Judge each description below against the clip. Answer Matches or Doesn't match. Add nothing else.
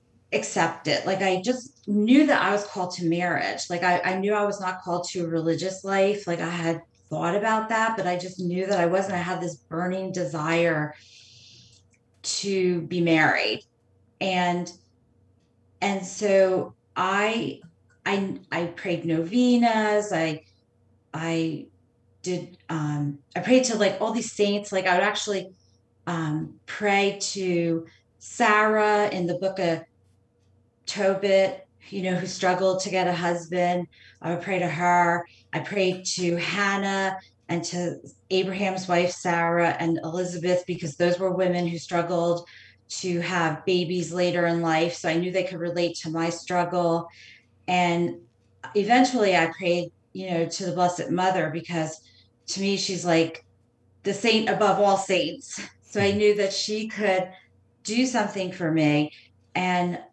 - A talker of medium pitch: Matches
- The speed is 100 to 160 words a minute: Matches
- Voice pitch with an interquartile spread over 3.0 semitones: Doesn't match